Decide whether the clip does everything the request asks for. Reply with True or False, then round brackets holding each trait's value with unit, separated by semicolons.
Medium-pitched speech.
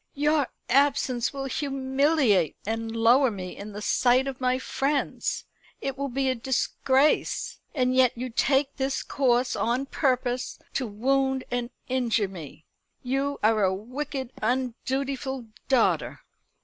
False (260 Hz)